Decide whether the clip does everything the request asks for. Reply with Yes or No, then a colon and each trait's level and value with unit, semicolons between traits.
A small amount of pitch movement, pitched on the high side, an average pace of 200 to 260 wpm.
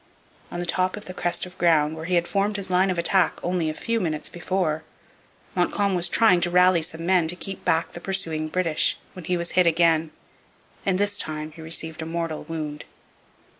No: narrow, 2.3 semitones; medium, 175 Hz; fast, 205 wpm